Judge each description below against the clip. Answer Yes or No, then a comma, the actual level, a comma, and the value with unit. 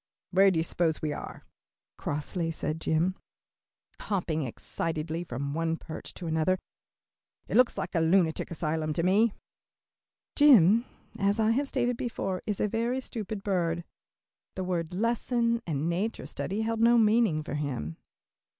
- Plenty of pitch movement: Yes, wide, 5.7 semitones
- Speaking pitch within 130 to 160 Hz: No, medium, 180 Hz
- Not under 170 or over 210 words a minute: No, average, 150 wpm